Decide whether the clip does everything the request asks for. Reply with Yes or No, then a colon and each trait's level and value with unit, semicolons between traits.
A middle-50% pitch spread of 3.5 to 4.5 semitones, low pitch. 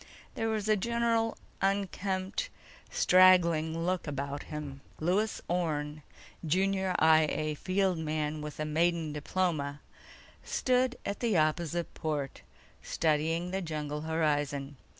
No: average, 3.9 semitones; medium, 165 Hz